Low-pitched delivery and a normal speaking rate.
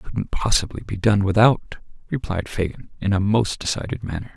Yes: low, 105 Hz; average, 180 wpm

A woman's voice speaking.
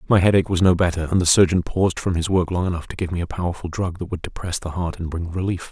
No: male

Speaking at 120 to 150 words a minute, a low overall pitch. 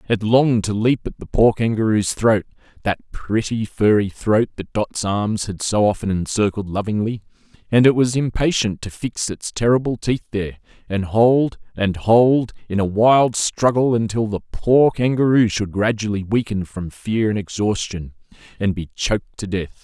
No: average, 165 wpm; low, 110 Hz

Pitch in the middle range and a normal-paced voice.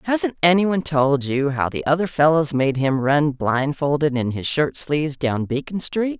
Yes: medium, 150 Hz; average, 185 wpm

